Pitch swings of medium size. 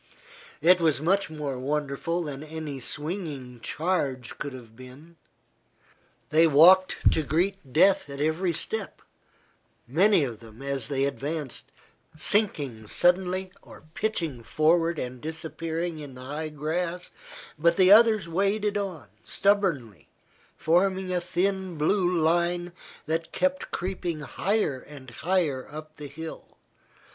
Yes: average, 4.5 semitones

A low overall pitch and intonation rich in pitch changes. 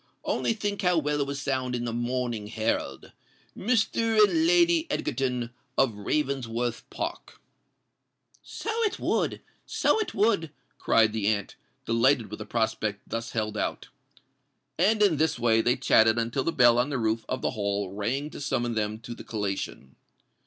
Yes: low, 120 Hz; wide, 6.2 semitones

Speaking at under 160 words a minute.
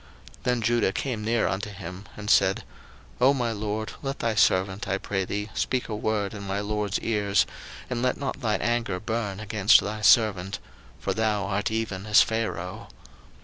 No: average, 180 wpm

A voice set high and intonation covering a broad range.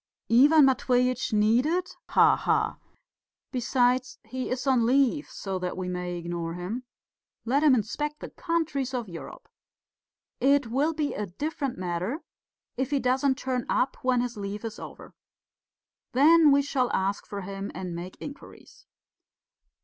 Yes: very high, 250 Hz; wide, 5.8 semitones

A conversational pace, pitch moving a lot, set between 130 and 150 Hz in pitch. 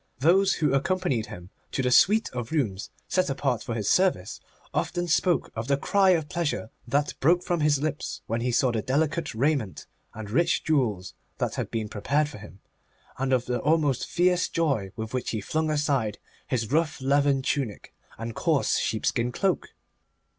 Yes: average, 175 wpm; wide, 5.7 semitones; medium, 140 Hz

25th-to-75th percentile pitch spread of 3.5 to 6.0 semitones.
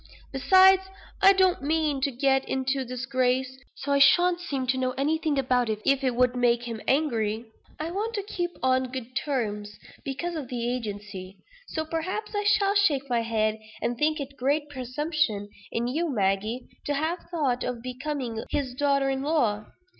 Yes: average, 4.2 semitones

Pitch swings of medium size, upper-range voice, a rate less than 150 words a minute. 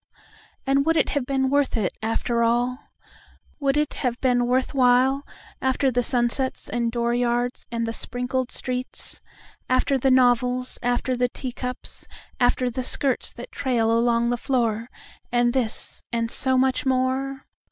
No: narrow, 1.6 semitones; very high, 250 Hz; average, 140 wpm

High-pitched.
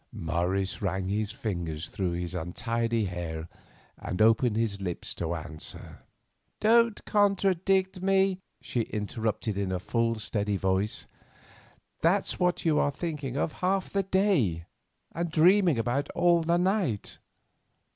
No: low, 115 Hz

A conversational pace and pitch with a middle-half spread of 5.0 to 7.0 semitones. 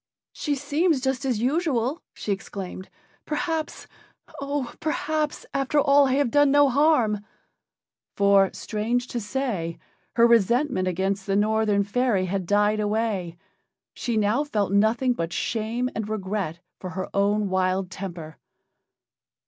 No: slow, 130 wpm; wide, 5.5 semitones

